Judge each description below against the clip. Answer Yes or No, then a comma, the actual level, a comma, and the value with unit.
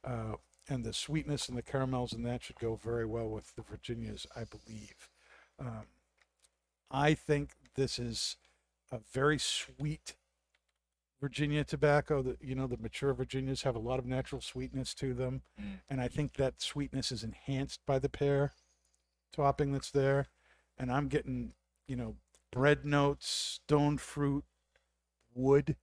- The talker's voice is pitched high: No, low, 130 Hz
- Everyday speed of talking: Yes, average, 150 wpm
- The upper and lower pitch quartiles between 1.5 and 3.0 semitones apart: No, average, 4.0 semitones